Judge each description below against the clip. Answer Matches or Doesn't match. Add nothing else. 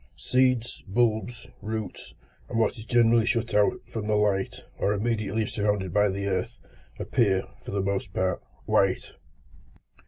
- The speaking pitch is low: Matches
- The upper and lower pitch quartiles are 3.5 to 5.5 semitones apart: Doesn't match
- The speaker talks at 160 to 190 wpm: Doesn't match